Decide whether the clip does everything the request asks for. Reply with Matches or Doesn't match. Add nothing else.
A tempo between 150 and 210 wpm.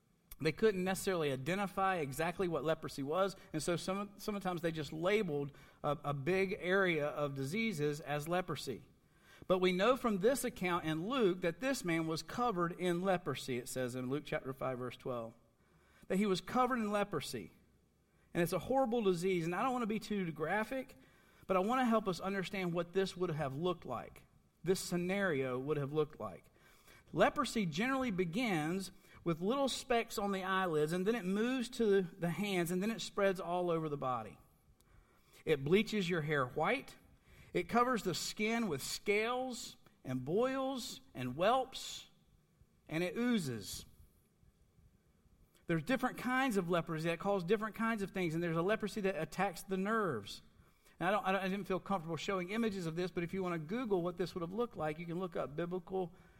Matches